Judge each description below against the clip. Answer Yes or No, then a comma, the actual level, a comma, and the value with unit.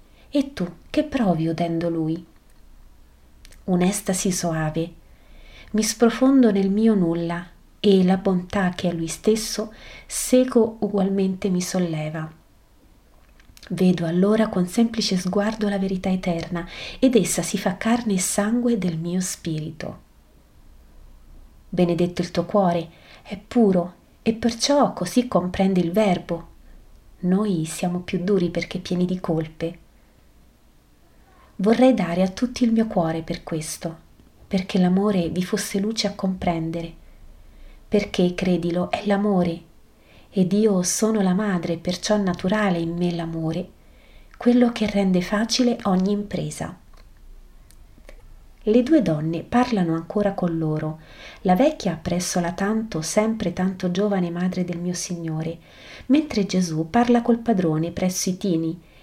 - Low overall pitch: No, medium, 185 Hz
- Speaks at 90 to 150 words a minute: Yes, average, 125 wpm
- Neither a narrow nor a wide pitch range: Yes, average, 3.5 semitones